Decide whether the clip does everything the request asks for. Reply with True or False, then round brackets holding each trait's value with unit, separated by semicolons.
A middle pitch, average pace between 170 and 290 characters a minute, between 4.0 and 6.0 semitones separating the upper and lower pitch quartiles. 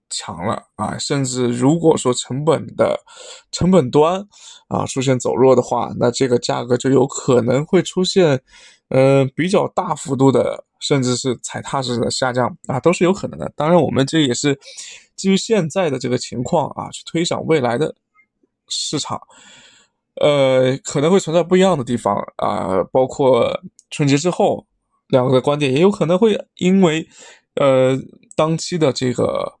True (145 Hz; 240 characters per minute; 5.6 semitones)